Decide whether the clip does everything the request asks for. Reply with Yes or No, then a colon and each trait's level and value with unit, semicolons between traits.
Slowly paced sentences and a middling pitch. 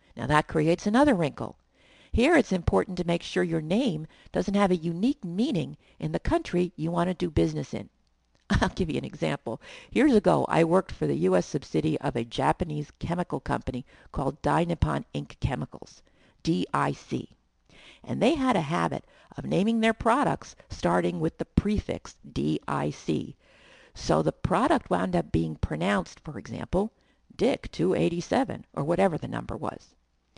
No: average, 155 wpm; medium, 165 Hz